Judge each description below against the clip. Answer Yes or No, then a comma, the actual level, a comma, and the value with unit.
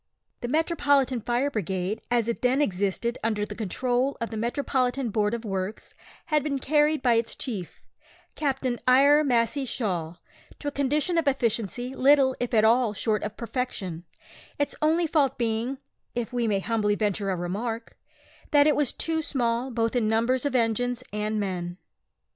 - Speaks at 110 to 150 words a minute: No, average, 165 wpm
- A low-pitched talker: No, high, 240 Hz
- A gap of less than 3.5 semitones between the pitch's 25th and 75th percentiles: No, average, 4.1 semitones